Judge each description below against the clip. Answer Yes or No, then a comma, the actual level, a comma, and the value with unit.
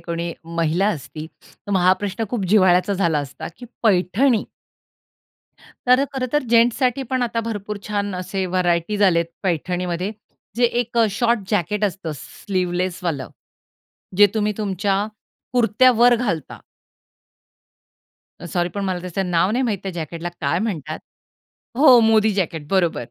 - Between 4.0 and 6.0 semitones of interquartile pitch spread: Yes, average, 4.3 semitones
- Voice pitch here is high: Yes, high, 195 Hz